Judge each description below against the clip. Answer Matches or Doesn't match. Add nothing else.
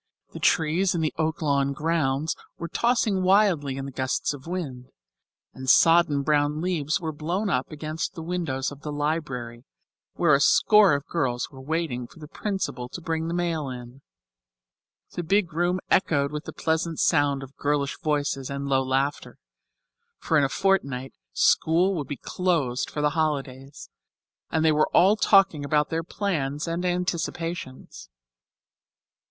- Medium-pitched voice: Matches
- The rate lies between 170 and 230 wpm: Doesn't match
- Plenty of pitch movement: Doesn't match